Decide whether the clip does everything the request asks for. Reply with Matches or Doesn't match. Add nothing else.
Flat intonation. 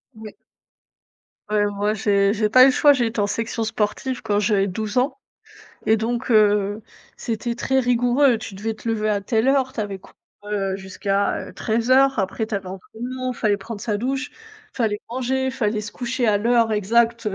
Doesn't match